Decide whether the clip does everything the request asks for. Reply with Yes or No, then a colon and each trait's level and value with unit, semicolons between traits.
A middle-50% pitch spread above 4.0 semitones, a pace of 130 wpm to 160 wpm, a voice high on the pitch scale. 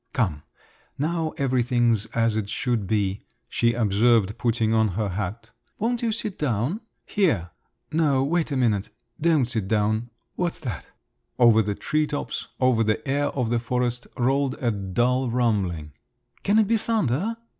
No: average, 4.9 semitones; average, 155 wpm; low, 120 Hz